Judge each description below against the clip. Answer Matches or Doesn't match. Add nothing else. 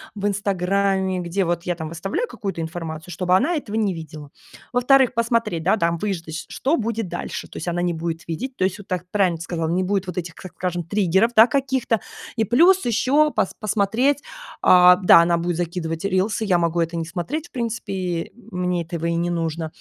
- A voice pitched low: Doesn't match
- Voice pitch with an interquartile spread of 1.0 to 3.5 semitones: Doesn't match